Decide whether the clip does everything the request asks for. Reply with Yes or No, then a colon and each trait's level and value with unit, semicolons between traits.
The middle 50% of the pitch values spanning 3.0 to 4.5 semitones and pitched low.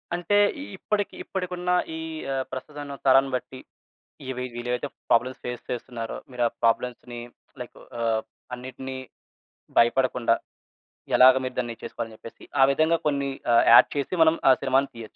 No: narrow, 2.6 semitones; low, 130 Hz